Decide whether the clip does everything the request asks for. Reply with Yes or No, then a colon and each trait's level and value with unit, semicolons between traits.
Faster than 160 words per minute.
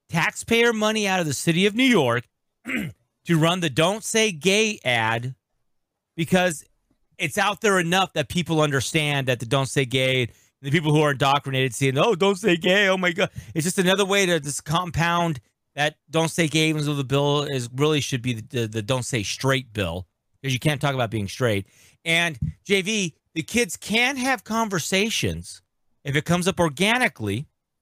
Yes: average, 185 wpm